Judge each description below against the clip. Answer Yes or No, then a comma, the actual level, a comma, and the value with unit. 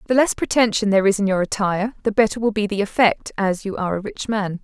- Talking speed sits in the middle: No, fast, 260 wpm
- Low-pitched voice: No, high, 210 Hz